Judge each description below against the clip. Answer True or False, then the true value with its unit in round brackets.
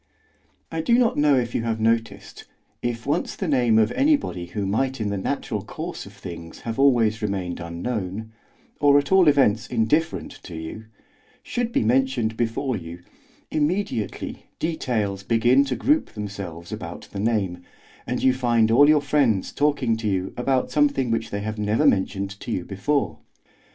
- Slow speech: False (165 wpm)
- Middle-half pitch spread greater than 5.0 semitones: True (5.6 semitones)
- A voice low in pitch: True (115 Hz)